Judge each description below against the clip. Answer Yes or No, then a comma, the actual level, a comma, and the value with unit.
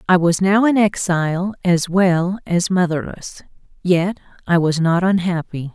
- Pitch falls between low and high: Yes, medium, 180 Hz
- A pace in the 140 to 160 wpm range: Yes, average, 145 wpm